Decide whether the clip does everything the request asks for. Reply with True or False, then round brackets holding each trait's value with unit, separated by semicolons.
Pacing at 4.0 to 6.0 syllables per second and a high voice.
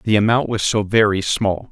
False (4.8 syllables/s; 105 Hz)